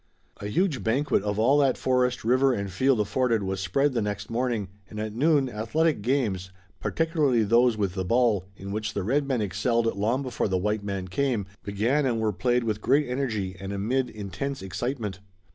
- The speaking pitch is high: No, low, 115 Hz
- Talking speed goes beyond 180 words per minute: Yes, average, 190 wpm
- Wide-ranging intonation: No, average, 4.4 semitones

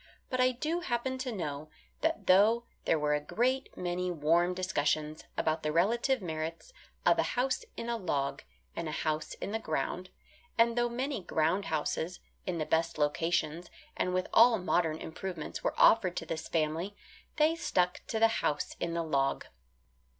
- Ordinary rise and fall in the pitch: No, wide, 6.7 semitones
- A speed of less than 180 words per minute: Yes, average, 170 wpm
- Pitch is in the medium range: Yes, medium, 180 Hz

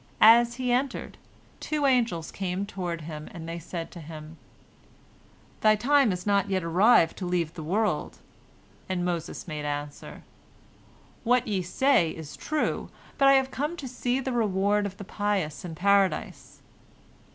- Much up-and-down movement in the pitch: Yes, wide, 6.3 semitones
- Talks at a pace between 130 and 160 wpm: Yes, average, 155 wpm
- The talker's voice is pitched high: Yes, high, 195 Hz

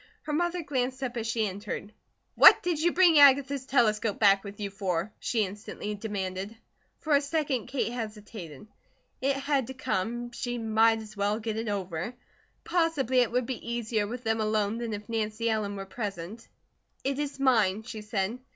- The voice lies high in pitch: Yes, high, 225 Hz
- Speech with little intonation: No, average, 4.0 semitones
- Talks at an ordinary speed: Yes, average, 180 wpm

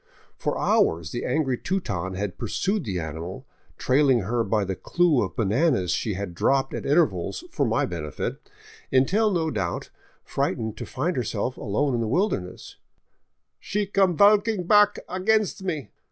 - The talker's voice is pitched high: No, low, 130 Hz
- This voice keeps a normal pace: Yes, average, 155 wpm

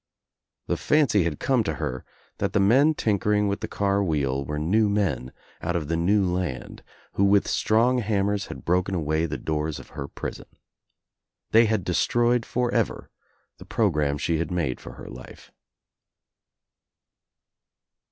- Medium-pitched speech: No, very low, 95 Hz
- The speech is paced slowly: No, average, 150 wpm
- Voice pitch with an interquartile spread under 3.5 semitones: No, wide, 5.4 semitones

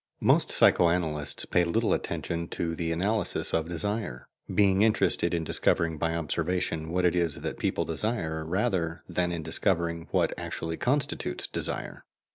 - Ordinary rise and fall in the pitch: No, narrow, 2.1 semitones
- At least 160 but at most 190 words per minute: No, average, 150 wpm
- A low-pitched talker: Yes, very low, 85 Hz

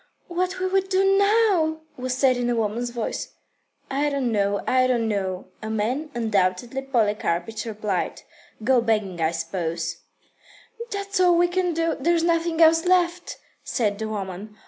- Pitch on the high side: Yes, very high, 250 Hz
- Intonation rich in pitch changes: Yes, wide, 8.4 semitones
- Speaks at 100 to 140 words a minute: No, average, 155 wpm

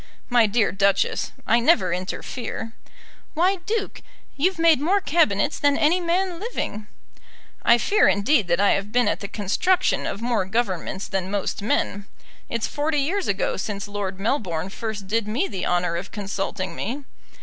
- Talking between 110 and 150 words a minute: No, average, 160 wpm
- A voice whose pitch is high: Yes, high, 225 Hz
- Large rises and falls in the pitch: Yes, wide, 7.7 semitones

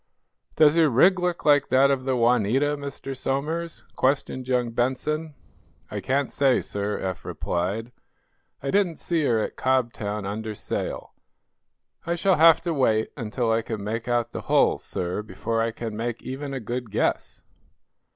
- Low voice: Yes, low, 130 Hz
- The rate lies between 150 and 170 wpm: Yes, average, 160 wpm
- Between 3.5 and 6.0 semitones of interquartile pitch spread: Yes, average, 4.4 semitones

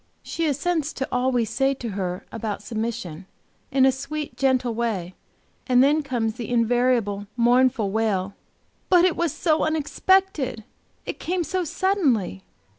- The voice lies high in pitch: Yes, very high, 250 Hz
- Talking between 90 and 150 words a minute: Yes, average, 145 wpm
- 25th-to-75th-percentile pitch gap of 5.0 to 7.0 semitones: Yes, average, 5.3 semitones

